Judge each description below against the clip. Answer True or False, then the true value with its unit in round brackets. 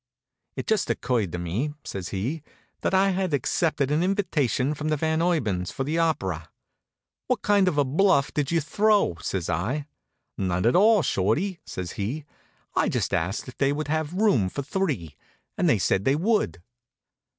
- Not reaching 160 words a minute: False (175 wpm)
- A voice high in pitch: False (145 Hz)